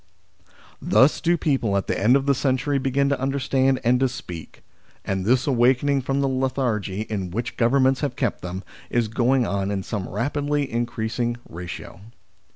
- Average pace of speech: Yes, average, 170 wpm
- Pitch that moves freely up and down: No, average, 3.8 semitones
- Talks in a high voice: No, low, 125 Hz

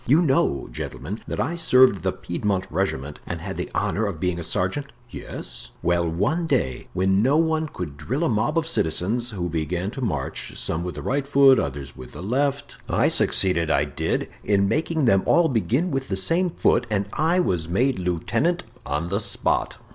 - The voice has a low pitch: Yes, low, 105 Hz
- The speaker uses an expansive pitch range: Yes, wide, 8.2 semitones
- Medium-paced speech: Yes, average, 195 wpm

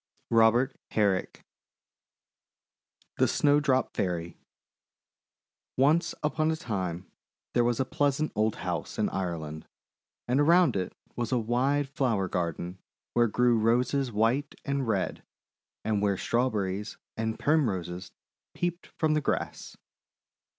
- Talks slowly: Yes, slow, 125 wpm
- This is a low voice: Yes, low, 120 Hz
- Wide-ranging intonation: Yes, wide, 6.3 semitones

